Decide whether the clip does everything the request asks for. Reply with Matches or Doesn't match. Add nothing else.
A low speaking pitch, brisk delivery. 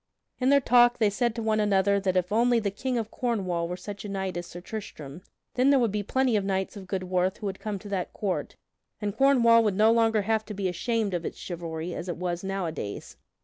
Doesn't match